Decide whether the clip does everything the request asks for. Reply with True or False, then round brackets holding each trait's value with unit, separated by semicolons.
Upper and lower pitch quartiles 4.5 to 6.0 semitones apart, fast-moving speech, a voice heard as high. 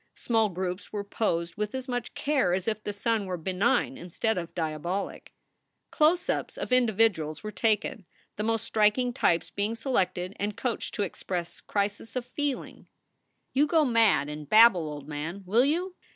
False (5.0 semitones; 170 wpm; 210 Hz)